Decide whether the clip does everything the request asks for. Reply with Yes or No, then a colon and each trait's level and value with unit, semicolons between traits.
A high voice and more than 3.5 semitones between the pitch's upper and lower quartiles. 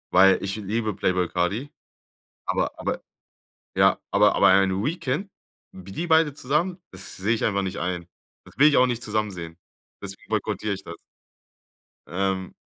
No: low, 100 Hz; average, 5.2 semitones